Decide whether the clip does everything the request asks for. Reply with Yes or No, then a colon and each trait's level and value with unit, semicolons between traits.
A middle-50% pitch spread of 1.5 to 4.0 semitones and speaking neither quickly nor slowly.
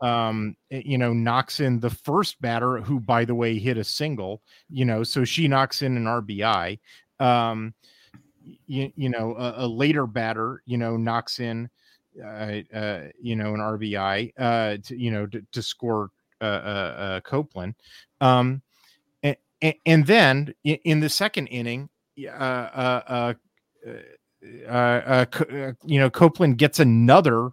Yes: average, 3.1 semitones; average, 155 wpm